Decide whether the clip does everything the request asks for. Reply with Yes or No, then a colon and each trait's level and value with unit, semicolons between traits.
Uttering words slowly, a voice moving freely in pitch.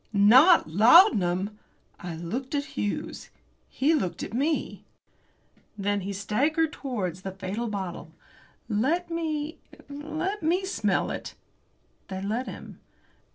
Yes: slow, 115 wpm; wide, 8.2 semitones